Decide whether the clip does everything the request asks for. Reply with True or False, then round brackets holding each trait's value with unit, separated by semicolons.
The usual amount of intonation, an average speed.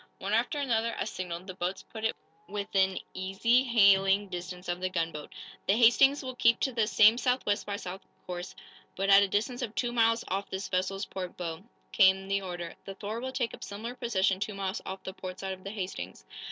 False (3.4 semitones; 215 wpm)